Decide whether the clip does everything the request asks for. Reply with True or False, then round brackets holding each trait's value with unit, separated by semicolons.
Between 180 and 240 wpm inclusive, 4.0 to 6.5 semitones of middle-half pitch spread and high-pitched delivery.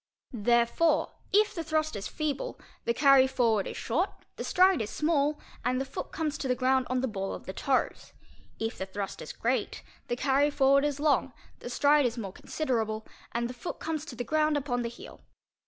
True (205 wpm; 4.3 semitones; 265 Hz)